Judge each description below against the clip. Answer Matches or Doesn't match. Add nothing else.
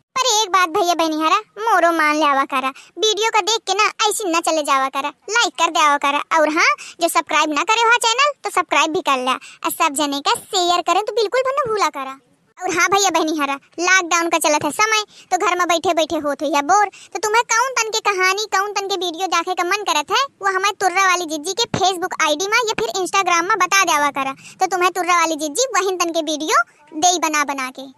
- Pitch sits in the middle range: Doesn't match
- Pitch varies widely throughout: Doesn't match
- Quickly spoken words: Matches